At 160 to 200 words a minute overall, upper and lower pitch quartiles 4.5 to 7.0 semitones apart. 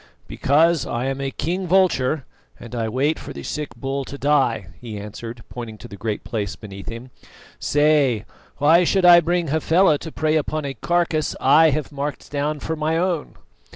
Yes: average, 185 wpm; average, 4.8 semitones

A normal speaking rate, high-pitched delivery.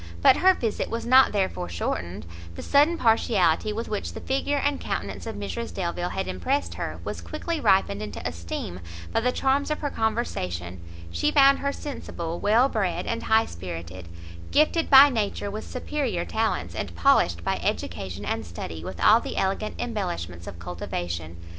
Yes: average, 170 wpm; high, 210 Hz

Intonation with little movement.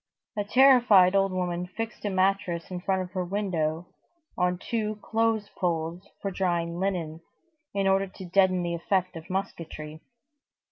Yes: narrow, 2.3 semitones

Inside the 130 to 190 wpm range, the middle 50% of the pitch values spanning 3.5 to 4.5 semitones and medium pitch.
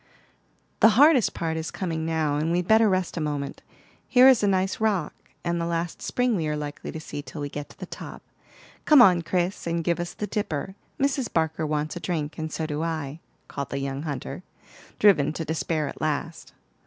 No: fast, 205 wpm; average, 3.8 semitones; medium, 165 Hz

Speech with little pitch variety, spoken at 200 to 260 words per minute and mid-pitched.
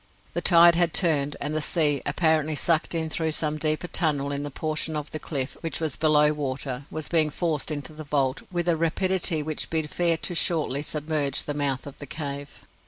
Yes: narrow, 2.0 semitones; fast, 205 wpm; medium, 155 Hz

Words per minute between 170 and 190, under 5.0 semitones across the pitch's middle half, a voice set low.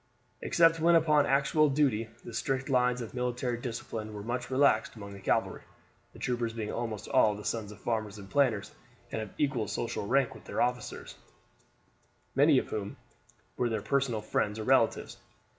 Yes: average, 175 wpm; average, 4.0 semitones; low, 120 Hz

